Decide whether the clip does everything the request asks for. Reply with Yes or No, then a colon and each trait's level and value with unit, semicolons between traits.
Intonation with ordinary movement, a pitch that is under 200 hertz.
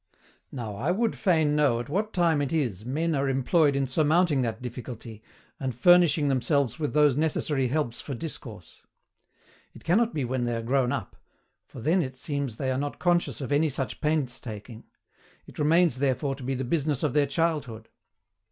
Yes: average, 4.0 semitones; medium, 140 Hz